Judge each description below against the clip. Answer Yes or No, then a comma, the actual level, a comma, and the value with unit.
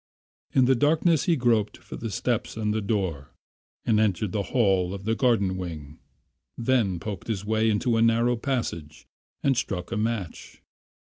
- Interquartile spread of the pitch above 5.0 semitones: No, average, 3.9 semitones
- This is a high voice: No, low, 110 Hz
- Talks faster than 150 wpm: Yes, average, 170 wpm